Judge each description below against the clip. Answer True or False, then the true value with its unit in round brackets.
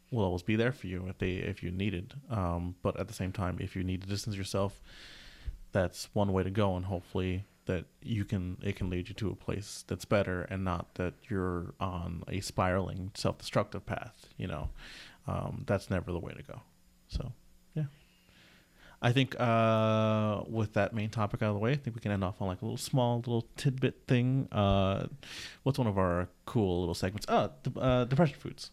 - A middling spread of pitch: True (3.8 semitones)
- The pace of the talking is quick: True (210 wpm)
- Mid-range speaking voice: False (100 Hz)